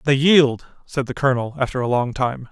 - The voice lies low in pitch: Yes, low, 130 Hz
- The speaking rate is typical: No, fast, 215 wpm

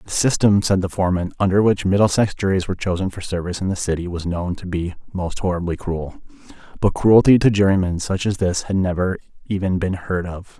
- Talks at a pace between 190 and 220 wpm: Yes, average, 200 wpm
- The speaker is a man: Yes, male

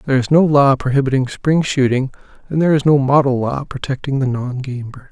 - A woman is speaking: No, male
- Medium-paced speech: No, fast, 210 wpm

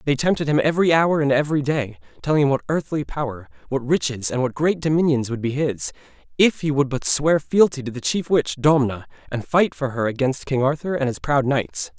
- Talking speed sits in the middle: No, fast, 220 wpm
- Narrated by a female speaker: No, male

